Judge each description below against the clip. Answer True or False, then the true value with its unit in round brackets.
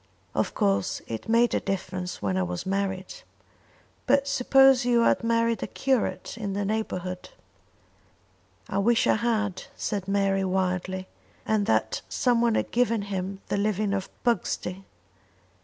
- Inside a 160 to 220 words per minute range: False (140 wpm)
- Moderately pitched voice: False (200 Hz)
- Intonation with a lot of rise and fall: False (3.7 semitones)